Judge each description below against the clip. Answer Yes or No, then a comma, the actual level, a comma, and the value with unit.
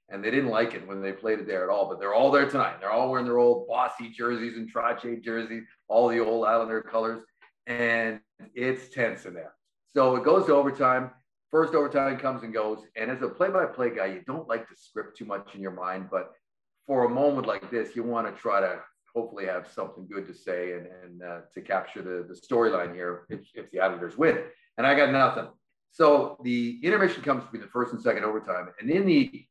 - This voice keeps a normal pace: No, fast, 225 wpm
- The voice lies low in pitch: Yes, low, 115 Hz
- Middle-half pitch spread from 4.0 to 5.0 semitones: Yes, average, 4.5 semitones